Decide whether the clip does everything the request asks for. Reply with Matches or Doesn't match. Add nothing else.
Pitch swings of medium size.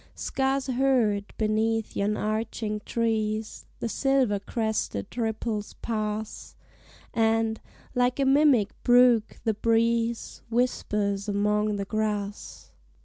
Doesn't match